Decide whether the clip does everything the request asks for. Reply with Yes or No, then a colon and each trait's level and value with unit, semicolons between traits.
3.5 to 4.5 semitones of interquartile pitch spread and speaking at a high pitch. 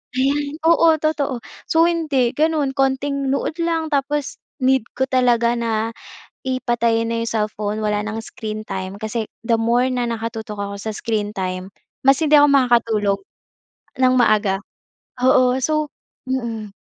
Yes: average, 4.2 semitones; high, 240 Hz